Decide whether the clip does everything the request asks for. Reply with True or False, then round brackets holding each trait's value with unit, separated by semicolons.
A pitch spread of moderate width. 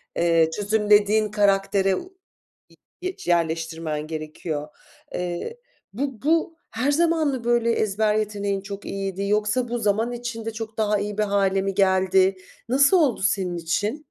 True (3.5 semitones)